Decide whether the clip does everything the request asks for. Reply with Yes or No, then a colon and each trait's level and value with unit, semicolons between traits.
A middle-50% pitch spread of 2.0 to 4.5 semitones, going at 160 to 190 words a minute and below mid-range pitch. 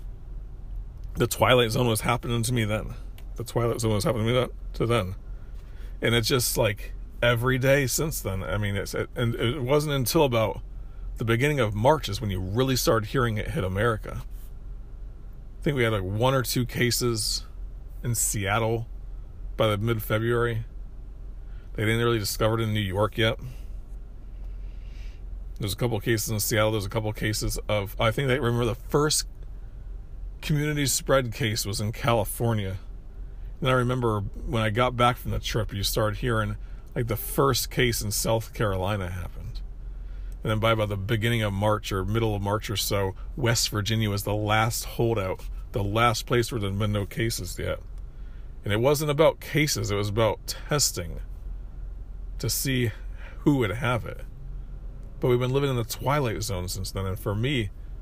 Yes: average, 3.0 semitones; average, 180 wpm; low, 115 Hz